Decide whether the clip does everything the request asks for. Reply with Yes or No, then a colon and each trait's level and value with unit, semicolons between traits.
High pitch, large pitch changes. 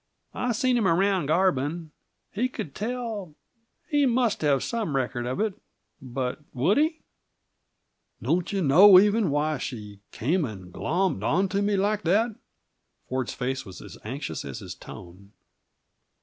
No: medium, 170 Hz; wide, 8.0 semitones